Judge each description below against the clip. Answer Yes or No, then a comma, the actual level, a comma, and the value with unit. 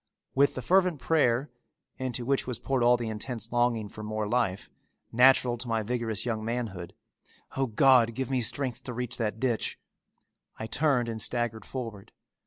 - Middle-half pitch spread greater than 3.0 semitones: No, average, 2.7 semitones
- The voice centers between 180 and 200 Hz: No, low, 120 Hz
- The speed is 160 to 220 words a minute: Yes, average, 170 wpm